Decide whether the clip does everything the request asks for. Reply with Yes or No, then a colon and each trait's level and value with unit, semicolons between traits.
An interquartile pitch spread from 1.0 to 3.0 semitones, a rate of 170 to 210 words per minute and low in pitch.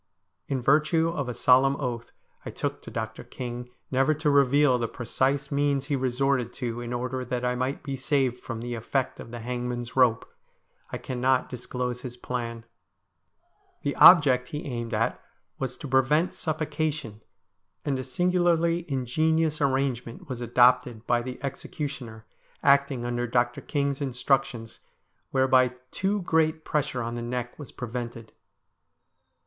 No: narrow, 2.6 semitones; average, 150 wpm; low, 130 Hz